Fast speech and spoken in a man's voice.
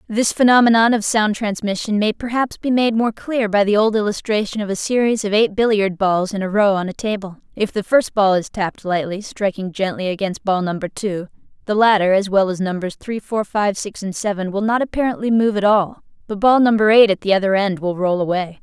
No: fast, 225 wpm; female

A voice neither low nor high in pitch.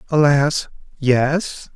Yes: medium, 145 Hz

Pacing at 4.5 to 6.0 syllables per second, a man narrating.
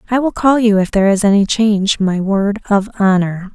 No: 5.5 syllables/s; female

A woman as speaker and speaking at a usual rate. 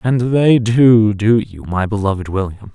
No: male; average, 175 wpm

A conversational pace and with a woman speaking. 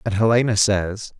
No: average, 150 wpm; male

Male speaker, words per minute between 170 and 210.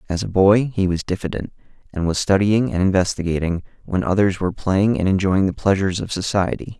Yes: male; average, 185 wpm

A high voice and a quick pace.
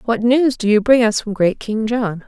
Yes: high, 225 Hz; fast, 265 wpm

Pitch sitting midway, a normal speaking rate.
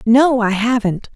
No: high, 235 Hz; average, 155 wpm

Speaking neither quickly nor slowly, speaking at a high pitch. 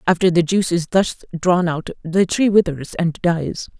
No: average, 190 wpm; medium, 175 Hz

